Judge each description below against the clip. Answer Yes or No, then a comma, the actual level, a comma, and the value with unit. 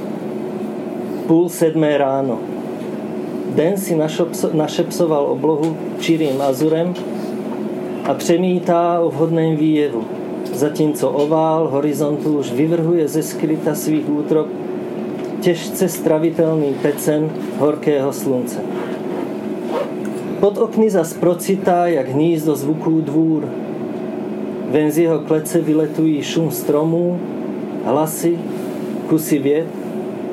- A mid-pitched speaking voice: Yes, medium, 160 Hz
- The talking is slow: Yes, slow, 90 wpm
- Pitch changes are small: Yes, narrow, 2.1 semitones